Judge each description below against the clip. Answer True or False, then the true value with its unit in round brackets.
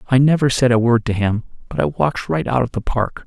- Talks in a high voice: False (120 Hz)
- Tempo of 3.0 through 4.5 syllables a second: False (5.6 syllables/s)